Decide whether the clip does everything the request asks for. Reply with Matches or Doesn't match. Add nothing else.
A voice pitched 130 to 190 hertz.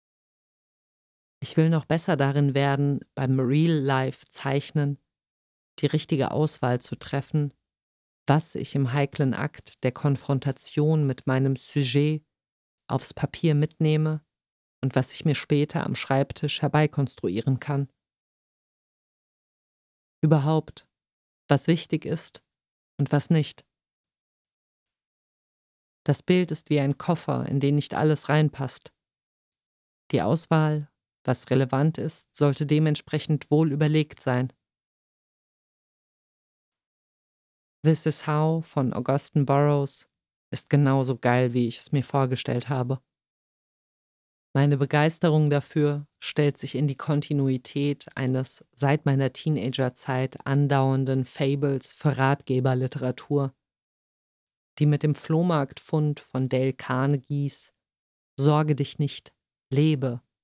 Matches